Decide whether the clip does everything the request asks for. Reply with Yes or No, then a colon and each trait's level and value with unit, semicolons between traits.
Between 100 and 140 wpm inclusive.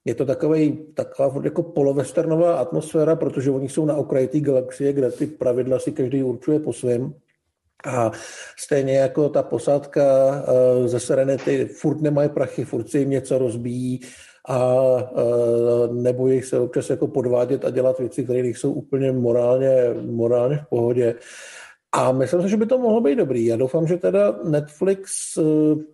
No: average, 160 wpm